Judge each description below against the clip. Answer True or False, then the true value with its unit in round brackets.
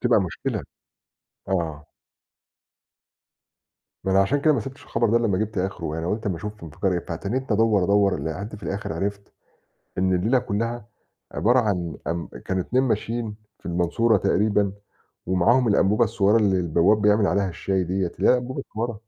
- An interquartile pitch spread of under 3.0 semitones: False (3.8 semitones)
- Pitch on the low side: True (100 Hz)